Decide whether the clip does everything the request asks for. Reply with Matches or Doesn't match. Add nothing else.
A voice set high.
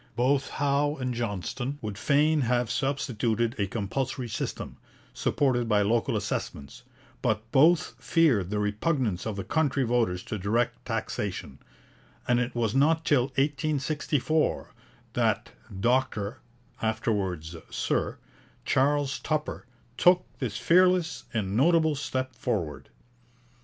Doesn't match